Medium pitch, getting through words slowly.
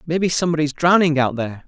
No: medium, 155 Hz; fast, 215 wpm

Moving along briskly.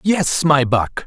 No: average, 170 wpm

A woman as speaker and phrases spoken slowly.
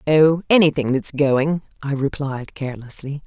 Yes: female; slow, 130 wpm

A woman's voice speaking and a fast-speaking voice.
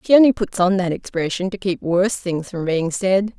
Yes: female; fast, 230 wpm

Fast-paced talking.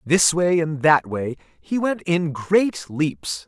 No: average, 175 wpm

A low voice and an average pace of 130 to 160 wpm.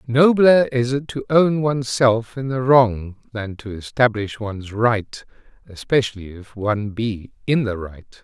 Yes: low, 115 Hz; average, 155 wpm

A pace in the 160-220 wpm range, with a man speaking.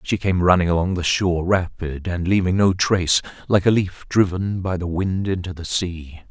Yes: average, 200 wpm; male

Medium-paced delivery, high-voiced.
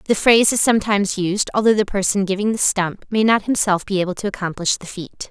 No: fast, 225 wpm; high, 200 Hz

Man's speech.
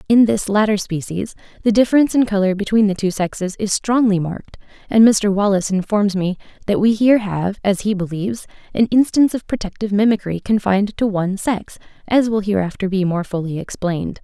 No: female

